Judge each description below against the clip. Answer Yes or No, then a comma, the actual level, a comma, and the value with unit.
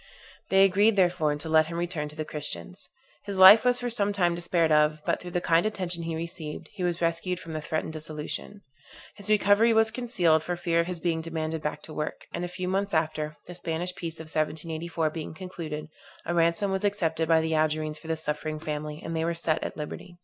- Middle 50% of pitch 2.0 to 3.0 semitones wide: Yes, narrow, 2.6 semitones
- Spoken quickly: Yes, fast, 220 wpm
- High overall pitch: No, medium, 165 Hz